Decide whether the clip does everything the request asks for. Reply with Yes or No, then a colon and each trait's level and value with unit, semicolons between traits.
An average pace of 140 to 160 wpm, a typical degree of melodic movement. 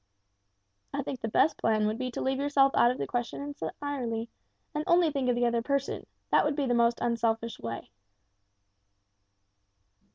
No: average, 170 wpm; average, 3.3 semitones